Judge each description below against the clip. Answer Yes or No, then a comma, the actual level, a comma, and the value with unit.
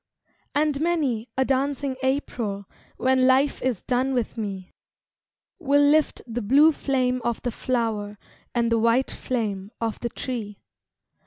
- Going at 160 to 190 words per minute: No, average, 140 wpm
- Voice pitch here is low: No, very high, 250 Hz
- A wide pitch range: No, average, 3.2 semitones